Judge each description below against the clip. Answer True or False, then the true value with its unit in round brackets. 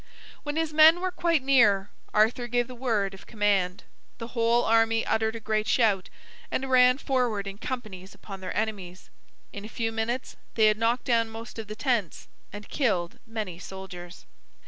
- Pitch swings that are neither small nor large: True (3.5 semitones)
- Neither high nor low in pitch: False (225 Hz)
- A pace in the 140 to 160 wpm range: False (175 wpm)